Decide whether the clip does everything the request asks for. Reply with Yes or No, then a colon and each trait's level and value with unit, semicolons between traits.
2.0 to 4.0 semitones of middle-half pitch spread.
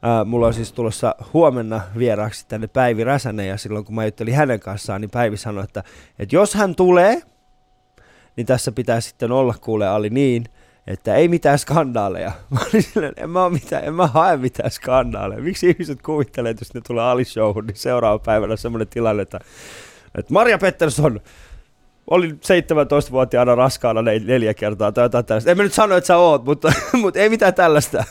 No: wide, 5.6 semitones